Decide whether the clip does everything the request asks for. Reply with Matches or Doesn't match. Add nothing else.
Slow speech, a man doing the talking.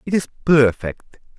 Matches